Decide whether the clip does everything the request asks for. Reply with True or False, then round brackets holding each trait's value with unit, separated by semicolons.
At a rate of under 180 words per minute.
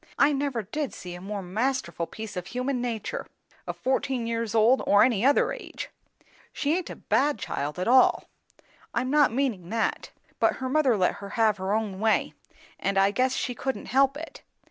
False (190 wpm)